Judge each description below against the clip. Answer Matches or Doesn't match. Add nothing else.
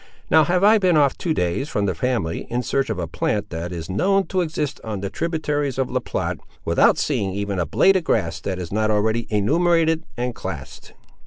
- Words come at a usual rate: Doesn't match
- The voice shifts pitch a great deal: Matches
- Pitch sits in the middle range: Doesn't match